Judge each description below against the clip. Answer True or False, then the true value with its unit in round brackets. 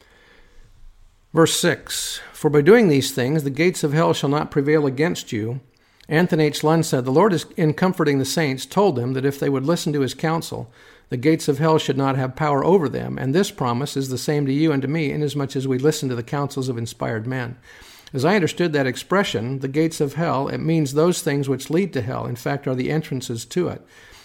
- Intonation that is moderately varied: True (3.4 semitones)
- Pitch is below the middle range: False (145 Hz)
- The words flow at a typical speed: False (230 wpm)